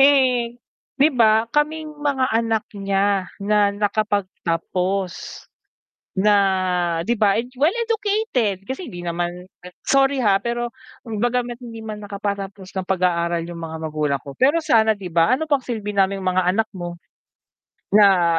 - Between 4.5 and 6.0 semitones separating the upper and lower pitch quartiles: Yes, average, 5.0 semitones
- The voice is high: Yes, high, 210 Hz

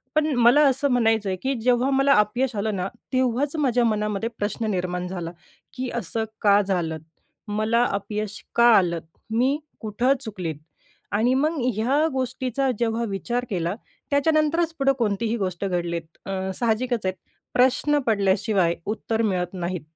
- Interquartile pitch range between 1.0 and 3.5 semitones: No, average, 4.7 semitones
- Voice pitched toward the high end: Yes, high, 225 Hz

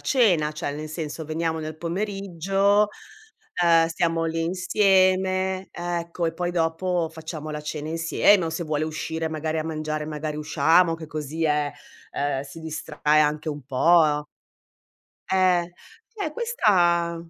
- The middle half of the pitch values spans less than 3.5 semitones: Yes, narrow, 2.6 semitones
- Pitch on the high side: No, medium, 165 Hz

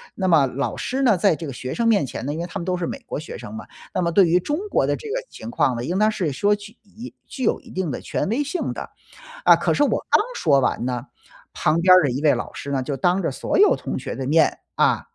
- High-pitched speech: No, medium, 175 Hz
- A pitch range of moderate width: No, wide, 7.1 semitones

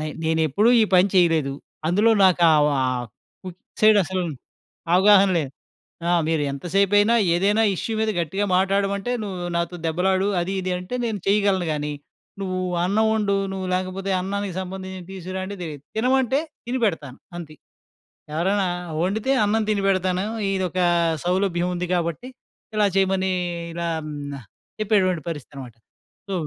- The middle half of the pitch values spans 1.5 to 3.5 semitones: Yes, average, 2.8 semitones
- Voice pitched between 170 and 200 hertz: Yes, medium, 185 Hz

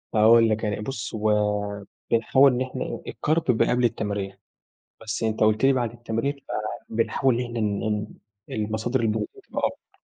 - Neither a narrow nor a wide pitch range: No, narrow, 2.3 semitones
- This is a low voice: Yes, low, 110 Hz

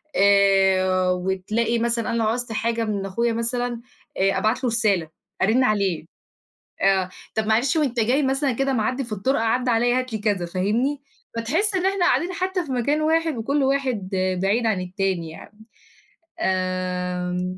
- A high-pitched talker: Yes, high, 225 Hz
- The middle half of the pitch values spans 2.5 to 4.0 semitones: No, average, 5.0 semitones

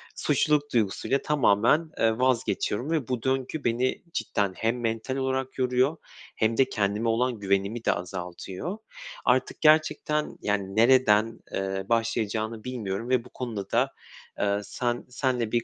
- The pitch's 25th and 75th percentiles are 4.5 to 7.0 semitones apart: No, average, 3.9 semitones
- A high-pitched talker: No, low, 115 Hz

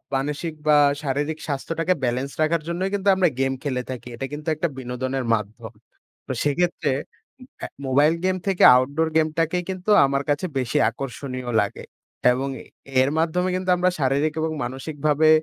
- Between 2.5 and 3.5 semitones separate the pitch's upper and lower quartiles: No, average, 3.9 semitones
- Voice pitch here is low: No, medium, 145 Hz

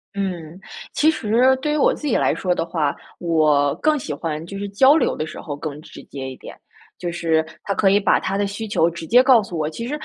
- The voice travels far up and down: Yes, wide, 6.5 semitones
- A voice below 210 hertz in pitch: Yes, high, 190 Hz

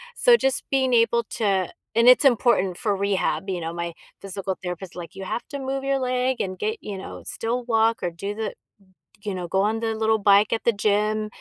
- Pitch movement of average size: Yes, average, 3.9 semitones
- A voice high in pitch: Yes, high, 215 Hz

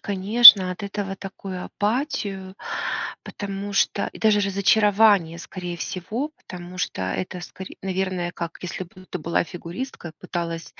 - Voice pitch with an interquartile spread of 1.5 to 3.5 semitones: Yes, narrow, 2.5 semitones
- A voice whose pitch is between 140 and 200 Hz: Yes, high, 190 Hz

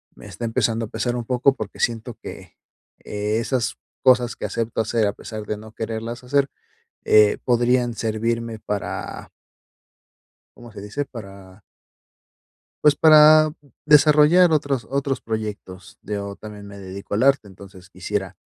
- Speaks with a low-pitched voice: Yes, low, 115 Hz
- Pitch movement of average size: Yes, average, 3.7 semitones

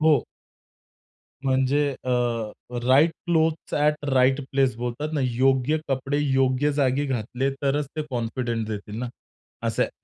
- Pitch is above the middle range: No, low, 135 Hz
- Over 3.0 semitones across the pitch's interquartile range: No, narrow, 2.5 semitones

